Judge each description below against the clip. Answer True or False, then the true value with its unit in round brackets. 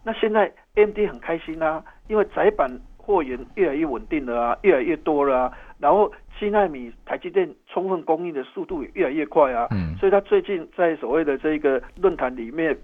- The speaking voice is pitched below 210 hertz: True (185 Hz)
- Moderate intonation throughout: False (7.4 semitones)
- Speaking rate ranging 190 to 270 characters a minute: False (305 characters per minute)